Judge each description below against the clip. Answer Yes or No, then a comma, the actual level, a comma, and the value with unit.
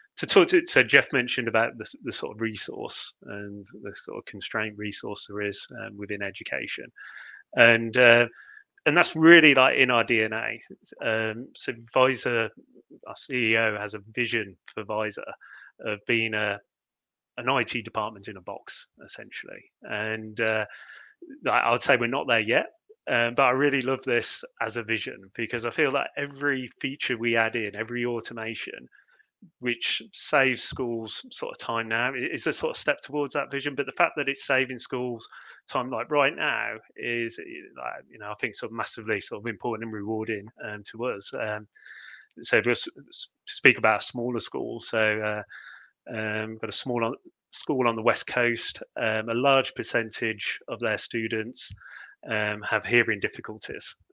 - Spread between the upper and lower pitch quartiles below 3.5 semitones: Yes, average, 3.1 semitones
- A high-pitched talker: No, low, 115 Hz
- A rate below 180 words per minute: Yes, average, 170 wpm